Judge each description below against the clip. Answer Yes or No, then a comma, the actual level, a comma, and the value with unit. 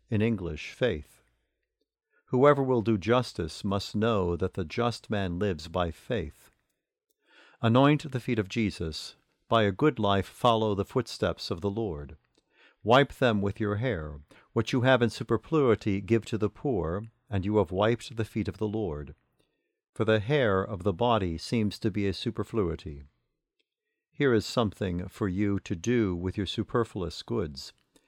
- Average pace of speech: Yes, average, 160 wpm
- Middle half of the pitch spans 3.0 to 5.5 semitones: Yes, average, 3.7 semitones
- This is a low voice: Yes, low, 105 Hz